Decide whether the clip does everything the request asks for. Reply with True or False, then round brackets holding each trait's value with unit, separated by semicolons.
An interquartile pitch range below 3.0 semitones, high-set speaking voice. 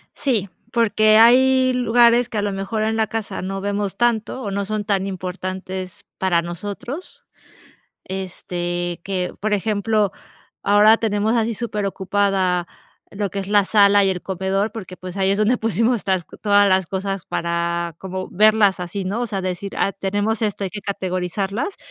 True (2.4 semitones; 200 Hz)